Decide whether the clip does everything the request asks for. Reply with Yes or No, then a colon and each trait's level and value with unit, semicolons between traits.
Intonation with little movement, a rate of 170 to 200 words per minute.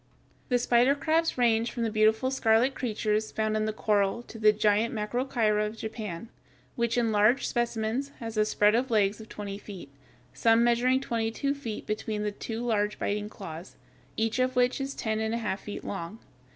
Yes: narrow, 2.2 semitones; average, 190 wpm